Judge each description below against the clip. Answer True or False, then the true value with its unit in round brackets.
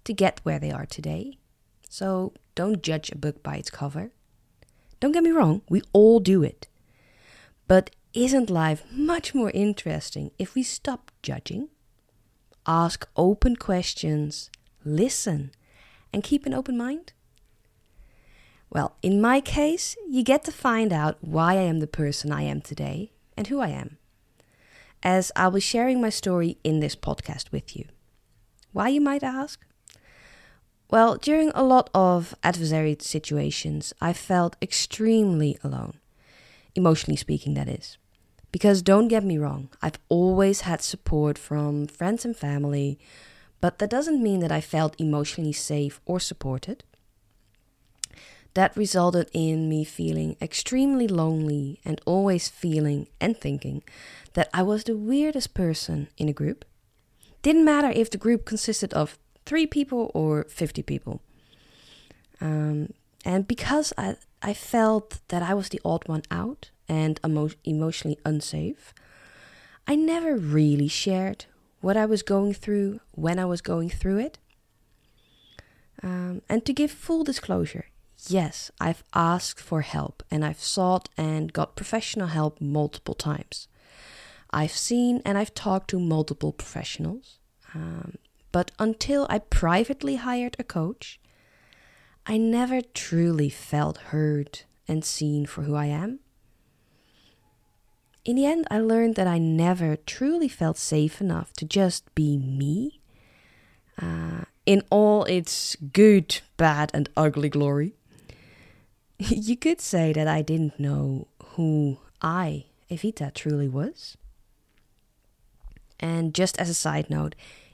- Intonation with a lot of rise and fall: True (6.5 semitones)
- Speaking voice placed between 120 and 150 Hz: False (165 Hz)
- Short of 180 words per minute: True (140 wpm)